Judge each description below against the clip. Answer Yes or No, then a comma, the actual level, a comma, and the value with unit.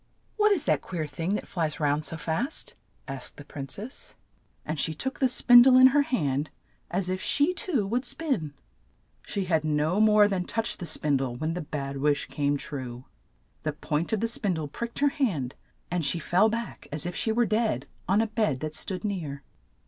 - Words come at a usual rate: No, fast, 215 wpm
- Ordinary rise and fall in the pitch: No, wide, 7.3 semitones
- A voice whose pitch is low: No, medium, 175 Hz